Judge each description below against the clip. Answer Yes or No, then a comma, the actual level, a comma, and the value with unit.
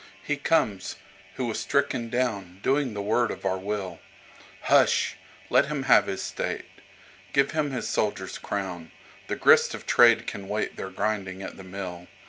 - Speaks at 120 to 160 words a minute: Yes, average, 140 wpm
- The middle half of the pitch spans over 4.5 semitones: Yes, average, 5.1 semitones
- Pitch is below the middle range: Yes, low, 100 Hz